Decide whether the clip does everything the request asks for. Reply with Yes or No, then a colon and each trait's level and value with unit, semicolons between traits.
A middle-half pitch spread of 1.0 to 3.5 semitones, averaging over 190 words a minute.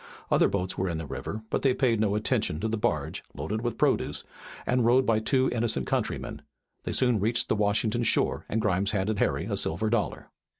Yes: average, 2.7 semitones; fast, 205 wpm